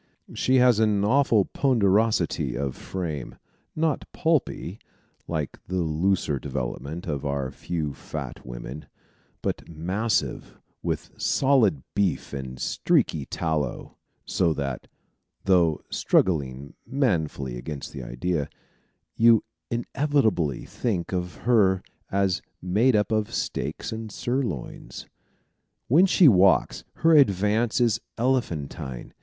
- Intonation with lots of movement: Yes, wide, 7.7 semitones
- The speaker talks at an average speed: No, slow, 110 wpm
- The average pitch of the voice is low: Yes, very low, 95 Hz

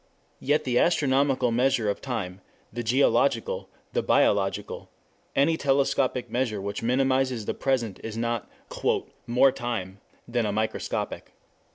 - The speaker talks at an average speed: No, slow, 125 wpm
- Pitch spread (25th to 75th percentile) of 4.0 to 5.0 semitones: No, average, 3.2 semitones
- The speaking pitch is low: Yes, low, 125 Hz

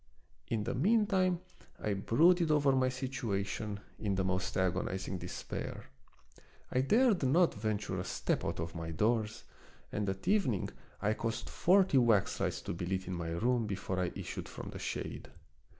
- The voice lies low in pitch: Yes, low, 110 Hz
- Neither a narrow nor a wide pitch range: No, wide, 6.4 semitones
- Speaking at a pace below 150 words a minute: No, average, 170 wpm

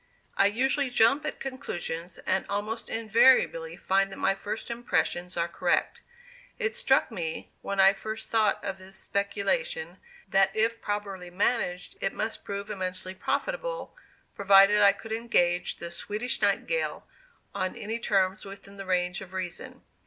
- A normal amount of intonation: Yes, average, 3.5 semitones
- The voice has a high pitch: Yes, high, 200 Hz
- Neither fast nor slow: Yes, average, 145 wpm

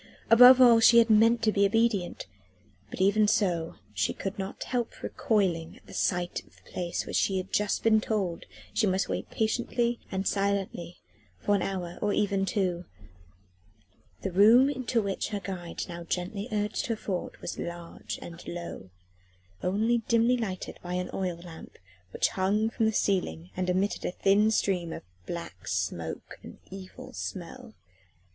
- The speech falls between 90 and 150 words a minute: No, average, 165 wpm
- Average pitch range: Yes, average, 3.7 semitones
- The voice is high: Yes, high, 195 Hz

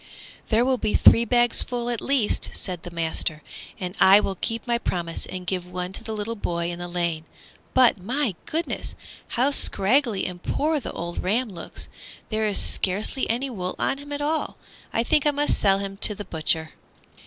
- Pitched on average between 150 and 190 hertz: No, high, 210 Hz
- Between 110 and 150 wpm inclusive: No, average, 195 wpm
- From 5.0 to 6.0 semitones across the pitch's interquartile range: Yes, wide, 5.5 semitones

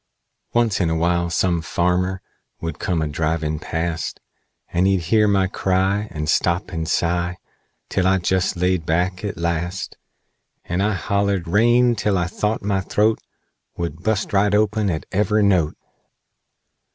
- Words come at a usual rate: Yes, average, 150 wpm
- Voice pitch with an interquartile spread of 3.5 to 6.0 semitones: No, average, 3.0 semitones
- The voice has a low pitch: Yes, very low, 90 Hz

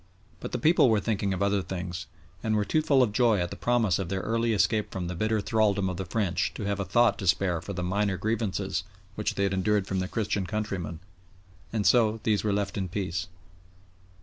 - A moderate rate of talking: No, fast, 225 wpm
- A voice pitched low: Yes, low, 100 Hz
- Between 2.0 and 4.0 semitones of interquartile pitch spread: Yes, average, 2.7 semitones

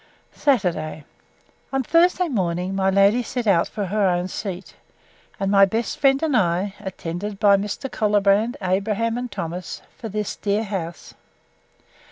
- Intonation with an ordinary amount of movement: Yes, average, 3.4 semitones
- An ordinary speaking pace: Yes, average, 145 wpm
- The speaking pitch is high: Yes, high, 200 Hz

